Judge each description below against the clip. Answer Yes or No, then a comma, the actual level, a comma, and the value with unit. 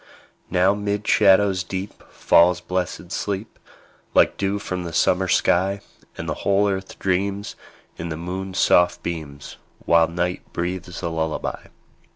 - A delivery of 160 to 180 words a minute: No, average, 140 wpm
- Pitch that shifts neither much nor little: No, narrow, 2.2 semitones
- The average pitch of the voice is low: Yes, very low, 90 Hz